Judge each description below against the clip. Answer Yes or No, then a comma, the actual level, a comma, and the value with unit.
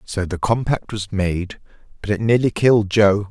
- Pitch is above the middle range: No, low, 105 Hz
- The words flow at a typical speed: Yes, average, 180 wpm